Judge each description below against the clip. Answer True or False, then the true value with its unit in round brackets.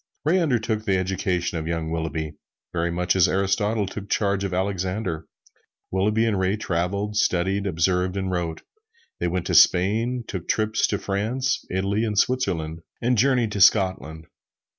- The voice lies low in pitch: True (95 Hz)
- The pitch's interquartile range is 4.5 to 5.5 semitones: False (3.3 semitones)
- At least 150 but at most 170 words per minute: True (155 wpm)